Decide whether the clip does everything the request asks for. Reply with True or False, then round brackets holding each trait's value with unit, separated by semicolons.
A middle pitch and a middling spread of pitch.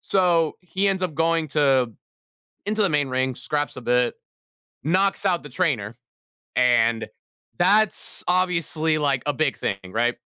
False (155 Hz; 6.0 semitones)